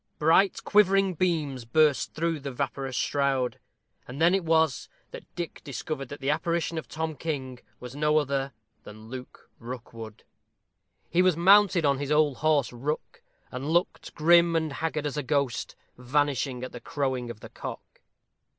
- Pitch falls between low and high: Yes, medium, 145 Hz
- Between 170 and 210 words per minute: No, average, 160 wpm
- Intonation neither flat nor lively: Yes, average, 3.7 semitones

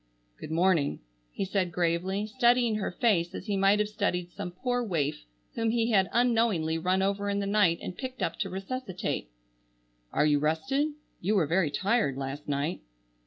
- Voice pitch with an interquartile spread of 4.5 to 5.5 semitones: Yes, average, 5.0 semitones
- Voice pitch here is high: Yes, high, 195 Hz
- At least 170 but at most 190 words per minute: Yes, average, 175 wpm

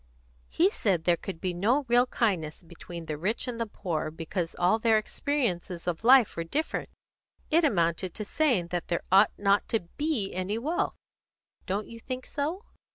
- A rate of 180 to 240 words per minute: No, average, 170 wpm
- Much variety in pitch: Yes, wide, 6.3 semitones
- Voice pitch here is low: No, high, 200 Hz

